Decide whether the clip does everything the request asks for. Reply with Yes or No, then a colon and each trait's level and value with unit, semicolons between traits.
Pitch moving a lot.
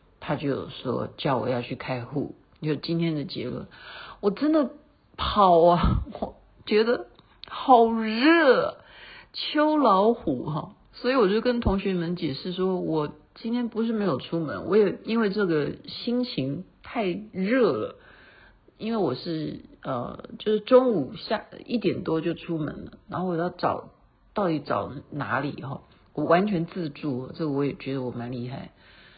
Yes: wide, 7.4 semitones